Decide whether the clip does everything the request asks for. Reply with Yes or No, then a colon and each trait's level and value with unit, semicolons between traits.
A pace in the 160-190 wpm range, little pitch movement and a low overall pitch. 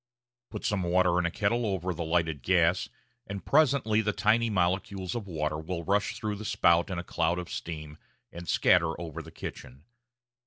No: average, 185 wpm; average, 3.6 semitones; very low, 90 Hz